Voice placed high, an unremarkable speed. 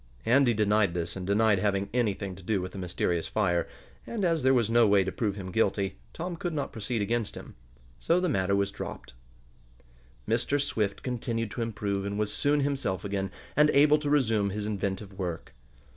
No: low, 105 Hz; average, 190 wpm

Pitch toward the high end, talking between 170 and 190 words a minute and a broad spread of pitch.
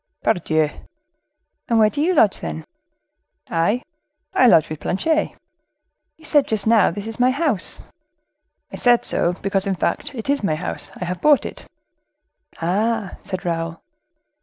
No: high, 210 Hz; average, 155 wpm; wide, 6.4 semitones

